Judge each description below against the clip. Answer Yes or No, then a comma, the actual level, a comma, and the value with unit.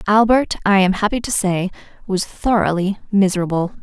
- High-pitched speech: Yes, high, 200 Hz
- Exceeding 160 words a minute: No, average, 140 wpm